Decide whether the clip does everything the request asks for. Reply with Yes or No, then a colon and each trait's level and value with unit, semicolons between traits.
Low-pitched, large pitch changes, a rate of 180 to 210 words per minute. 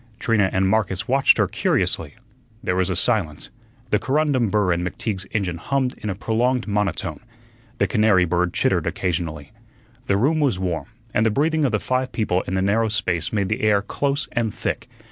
No: low, 105 Hz; average, 4.8 semitones; average, 185 wpm